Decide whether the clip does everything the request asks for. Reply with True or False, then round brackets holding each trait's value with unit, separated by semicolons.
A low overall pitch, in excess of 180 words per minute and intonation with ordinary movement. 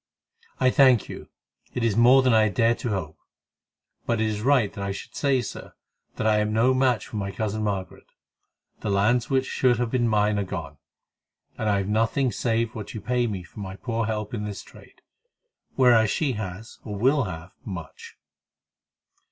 True (110 Hz; 190 wpm; 3.1 semitones)